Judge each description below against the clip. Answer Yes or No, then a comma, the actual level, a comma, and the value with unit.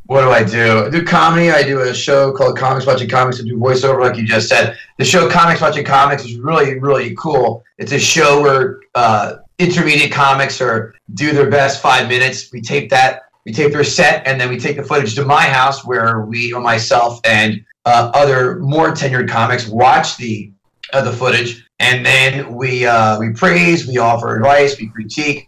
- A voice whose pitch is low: Yes, low, 130 Hz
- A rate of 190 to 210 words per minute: Yes, fast, 205 wpm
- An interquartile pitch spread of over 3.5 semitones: No, average, 3.2 semitones